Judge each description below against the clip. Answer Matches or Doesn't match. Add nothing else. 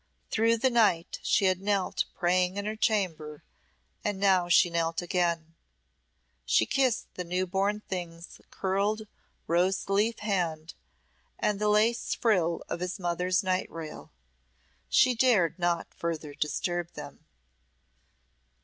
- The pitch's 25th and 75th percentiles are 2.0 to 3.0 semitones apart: Doesn't match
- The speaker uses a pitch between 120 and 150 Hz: Doesn't match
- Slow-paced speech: Matches